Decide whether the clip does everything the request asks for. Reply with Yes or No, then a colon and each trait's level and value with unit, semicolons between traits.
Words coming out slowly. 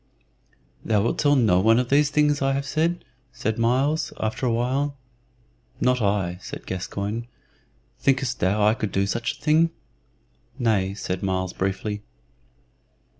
No: average, 150 wpm